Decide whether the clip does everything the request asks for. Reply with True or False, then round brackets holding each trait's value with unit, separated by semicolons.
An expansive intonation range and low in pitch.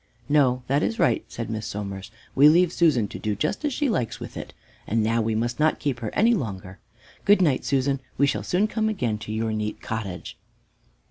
True (6.4 semitones; 125 Hz)